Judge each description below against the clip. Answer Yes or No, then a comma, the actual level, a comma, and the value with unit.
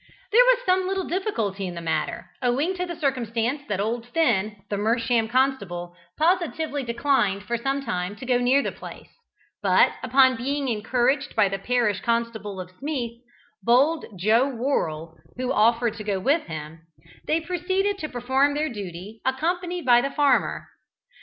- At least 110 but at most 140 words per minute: No, average, 160 wpm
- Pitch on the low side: No, high, 245 Hz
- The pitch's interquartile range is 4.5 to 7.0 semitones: Yes, wide, 5.5 semitones